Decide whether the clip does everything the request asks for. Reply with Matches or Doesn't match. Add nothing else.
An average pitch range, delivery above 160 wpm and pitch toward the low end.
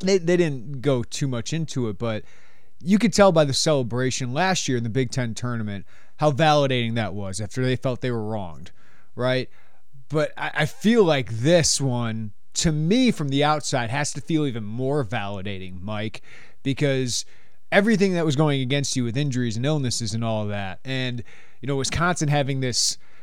Matches